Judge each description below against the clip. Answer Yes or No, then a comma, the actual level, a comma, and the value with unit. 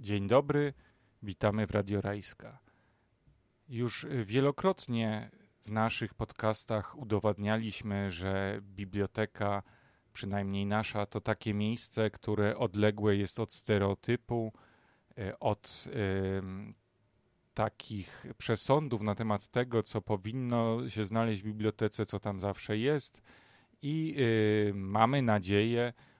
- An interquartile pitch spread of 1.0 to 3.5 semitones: Yes, narrow, 2.5 semitones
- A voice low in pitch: Yes, low, 110 Hz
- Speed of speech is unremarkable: No, slow, 105 wpm